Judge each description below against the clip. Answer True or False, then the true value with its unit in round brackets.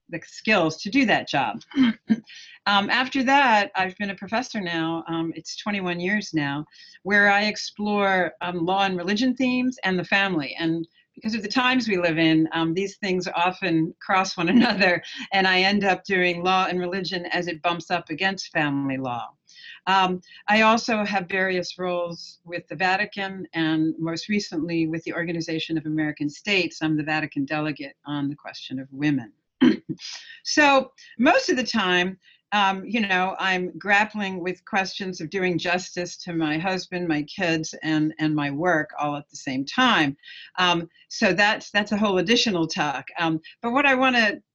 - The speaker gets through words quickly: False (175 wpm)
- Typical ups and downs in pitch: True (4.1 semitones)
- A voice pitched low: False (185 Hz)